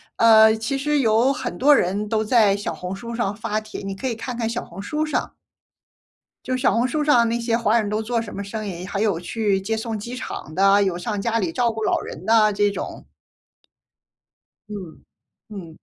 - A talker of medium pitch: No, high, 220 Hz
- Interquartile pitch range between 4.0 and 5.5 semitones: No, average, 2.8 semitones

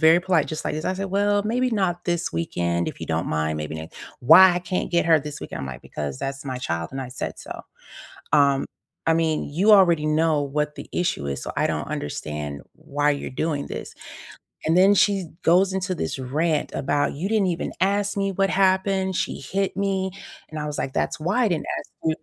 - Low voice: No, medium, 160 Hz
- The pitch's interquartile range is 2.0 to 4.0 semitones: No, wide, 5.6 semitones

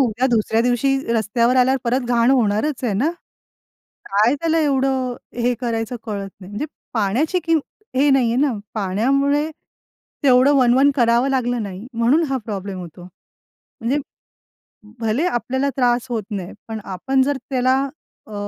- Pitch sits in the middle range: No, high, 245 Hz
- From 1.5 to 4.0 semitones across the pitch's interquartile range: Yes, average, 3.4 semitones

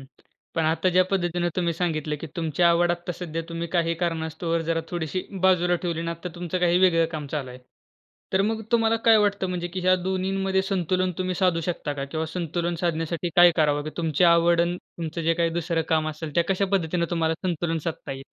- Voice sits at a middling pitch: Yes, medium, 170 Hz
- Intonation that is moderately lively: No, narrow, 1.9 semitones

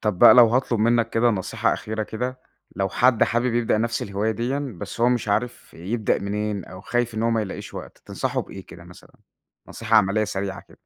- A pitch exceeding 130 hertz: No, low, 110 Hz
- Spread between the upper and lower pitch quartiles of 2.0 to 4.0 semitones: Yes, narrow, 2.5 semitones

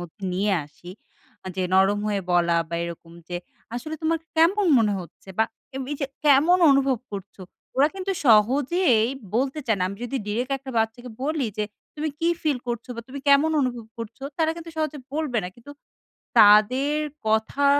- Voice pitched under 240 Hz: No, very high, 250 Hz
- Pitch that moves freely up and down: Yes, wide, 5.9 semitones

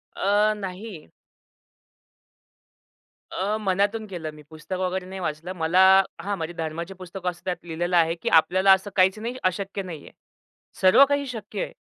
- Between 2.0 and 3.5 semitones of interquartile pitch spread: Yes, average, 2.9 semitones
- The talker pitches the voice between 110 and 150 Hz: No, medium, 185 Hz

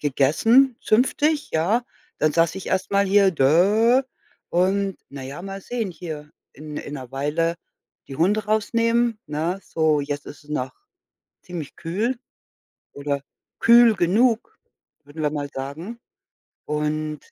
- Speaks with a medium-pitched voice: Yes, medium, 170 Hz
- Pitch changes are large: Yes, wide, 6.4 semitones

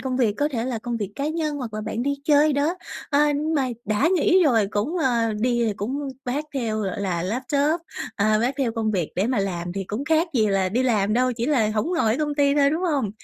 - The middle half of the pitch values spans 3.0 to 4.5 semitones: No, average, 5.2 semitones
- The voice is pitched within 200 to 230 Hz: No, very high, 250 Hz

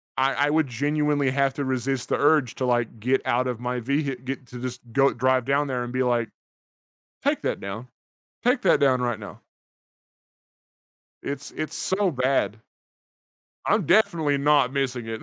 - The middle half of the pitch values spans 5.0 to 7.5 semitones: No, narrow, 2.6 semitones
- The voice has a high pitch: No, low, 130 Hz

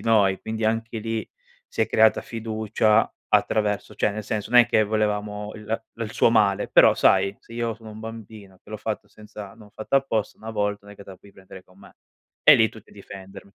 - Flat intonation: Yes, narrow, 1.6 semitones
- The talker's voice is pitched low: Yes, low, 110 Hz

